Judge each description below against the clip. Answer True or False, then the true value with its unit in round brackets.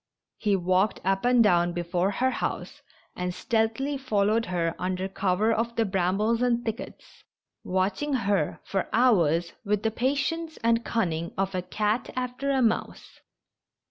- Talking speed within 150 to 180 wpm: True (160 wpm)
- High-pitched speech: True (210 Hz)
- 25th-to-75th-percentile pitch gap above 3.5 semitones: True (4.4 semitones)